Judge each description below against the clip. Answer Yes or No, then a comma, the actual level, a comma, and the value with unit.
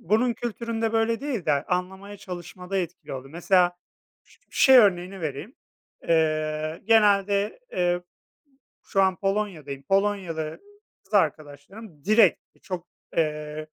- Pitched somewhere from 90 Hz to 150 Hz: No, medium, 185 Hz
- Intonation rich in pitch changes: No, average, 4.8 semitones